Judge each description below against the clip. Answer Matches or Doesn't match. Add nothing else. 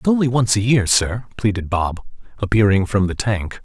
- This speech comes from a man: Matches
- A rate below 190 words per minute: Doesn't match